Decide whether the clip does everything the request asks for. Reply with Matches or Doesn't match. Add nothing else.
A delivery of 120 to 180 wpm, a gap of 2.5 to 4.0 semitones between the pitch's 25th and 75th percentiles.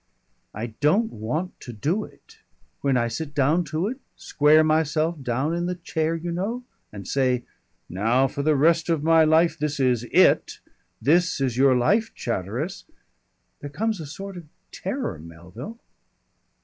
Doesn't match